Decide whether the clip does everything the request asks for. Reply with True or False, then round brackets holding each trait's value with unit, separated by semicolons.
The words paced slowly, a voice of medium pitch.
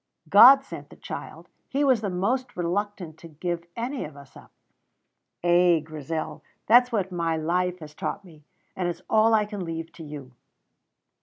False (165 wpm; 180 Hz)